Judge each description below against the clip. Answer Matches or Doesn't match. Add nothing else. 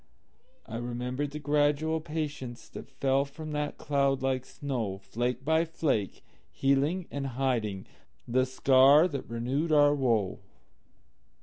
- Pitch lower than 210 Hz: Matches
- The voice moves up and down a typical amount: Matches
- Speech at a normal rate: Doesn't match